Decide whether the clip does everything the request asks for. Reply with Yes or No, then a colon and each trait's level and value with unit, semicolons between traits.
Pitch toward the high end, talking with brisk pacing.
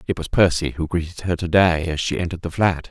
No: very low, 85 Hz; fast, 270 wpm